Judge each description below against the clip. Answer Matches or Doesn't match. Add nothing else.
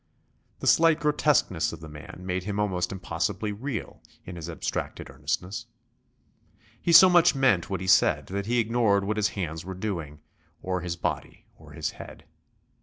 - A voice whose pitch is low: Matches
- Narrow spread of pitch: Doesn't match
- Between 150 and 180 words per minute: Matches